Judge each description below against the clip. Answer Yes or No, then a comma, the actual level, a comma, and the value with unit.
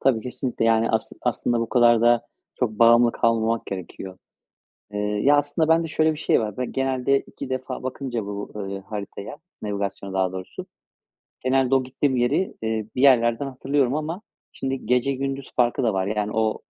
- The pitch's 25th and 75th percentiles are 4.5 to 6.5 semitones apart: No, average, 3.8 semitones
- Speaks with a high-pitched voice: No, low, 120 Hz